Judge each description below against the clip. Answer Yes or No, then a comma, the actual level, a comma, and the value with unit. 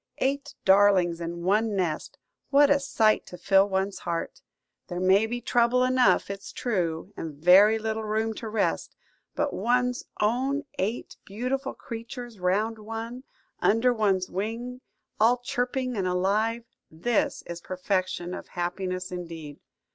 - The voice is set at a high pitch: Yes, high, 215 Hz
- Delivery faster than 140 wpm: No, slow, 135 wpm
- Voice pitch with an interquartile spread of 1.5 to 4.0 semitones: No, average, 4.7 semitones